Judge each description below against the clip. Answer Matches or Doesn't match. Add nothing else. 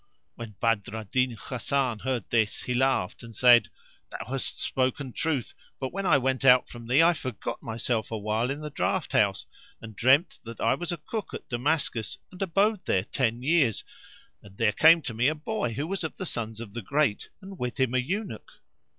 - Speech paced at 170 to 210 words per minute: Matches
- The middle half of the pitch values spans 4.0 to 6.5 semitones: Matches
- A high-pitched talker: Doesn't match